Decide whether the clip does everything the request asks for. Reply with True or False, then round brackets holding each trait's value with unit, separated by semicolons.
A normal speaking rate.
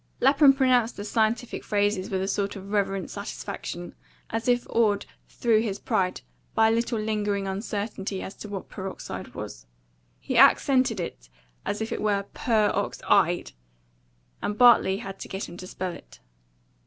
True (165 wpm)